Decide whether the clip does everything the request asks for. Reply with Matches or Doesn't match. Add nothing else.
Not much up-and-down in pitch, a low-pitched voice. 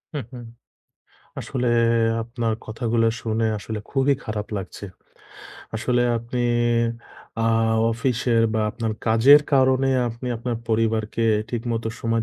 Matches